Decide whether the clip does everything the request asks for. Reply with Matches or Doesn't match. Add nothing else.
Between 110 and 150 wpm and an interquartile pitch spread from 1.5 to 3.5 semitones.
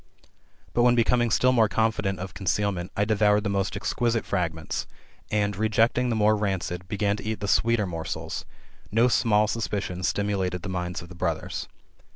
Doesn't match